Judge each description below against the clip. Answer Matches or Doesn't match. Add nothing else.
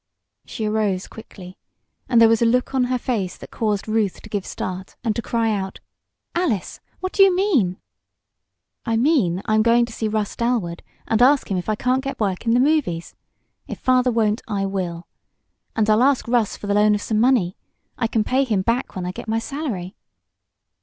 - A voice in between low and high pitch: Doesn't match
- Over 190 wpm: Matches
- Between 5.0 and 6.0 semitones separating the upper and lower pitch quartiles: Doesn't match